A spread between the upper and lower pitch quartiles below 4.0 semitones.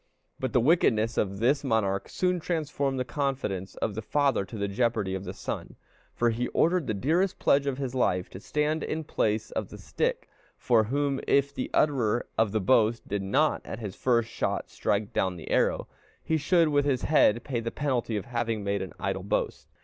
No: average, 5.0 semitones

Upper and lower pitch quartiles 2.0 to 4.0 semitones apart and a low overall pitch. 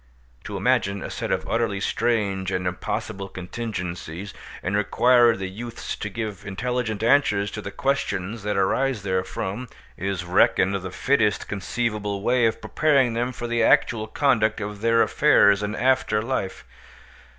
Yes: average, 3.3 semitones; low, 105 Hz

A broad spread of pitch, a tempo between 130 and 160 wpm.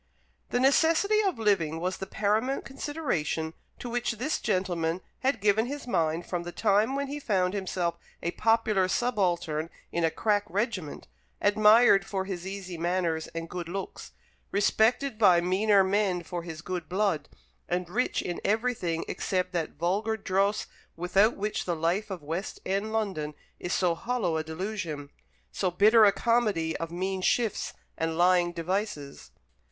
No: average, 4.1 semitones; average, 155 wpm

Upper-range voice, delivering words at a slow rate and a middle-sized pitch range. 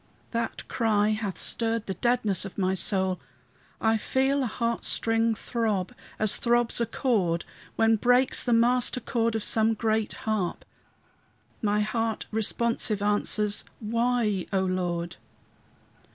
No: high, 220 Hz; slow, 130 wpm; narrow, 2.3 semitones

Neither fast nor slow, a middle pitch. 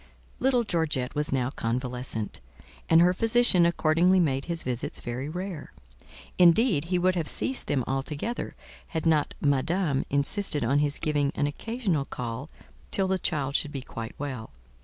Yes: average, 155 wpm; medium, 150 Hz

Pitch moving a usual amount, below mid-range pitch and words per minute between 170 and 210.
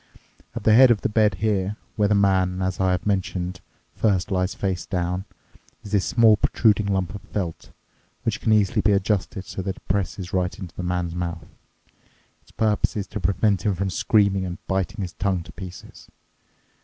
No: narrow, 2.1 semitones; very low, 95 Hz; average, 185 wpm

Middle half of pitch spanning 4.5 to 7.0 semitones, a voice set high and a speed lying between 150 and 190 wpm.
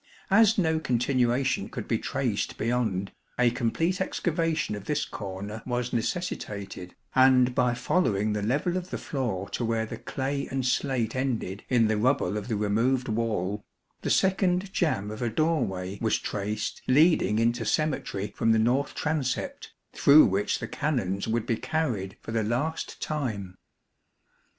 No: average, 5.2 semitones; low, 120 Hz; average, 155 wpm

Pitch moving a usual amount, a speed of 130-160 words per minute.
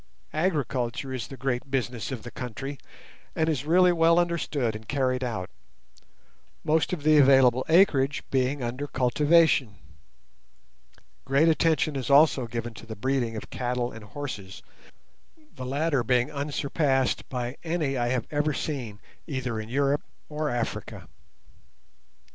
Yes: average, 3.5 semitones; slow, 135 wpm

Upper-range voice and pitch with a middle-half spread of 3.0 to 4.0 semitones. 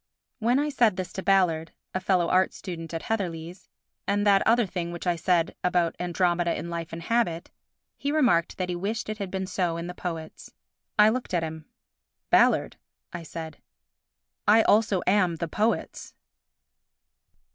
No: medium, 180 Hz; average, 3.4 semitones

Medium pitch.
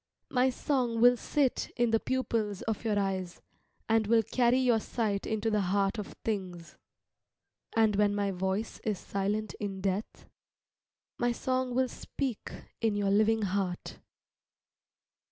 No: high, 215 Hz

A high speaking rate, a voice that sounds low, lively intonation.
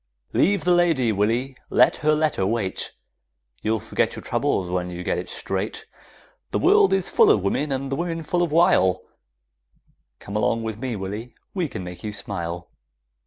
No: average, 175 wpm; low, 115 Hz; wide, 8.3 semitones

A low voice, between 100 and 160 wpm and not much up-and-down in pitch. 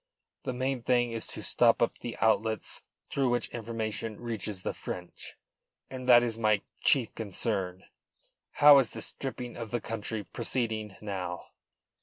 Yes: low, 115 Hz; average, 150 wpm; narrow, 2.2 semitones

